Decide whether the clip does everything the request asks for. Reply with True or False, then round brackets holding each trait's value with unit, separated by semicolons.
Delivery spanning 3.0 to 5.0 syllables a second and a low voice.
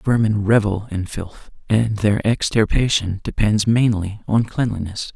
True (4.1 syllables/s; 105 Hz)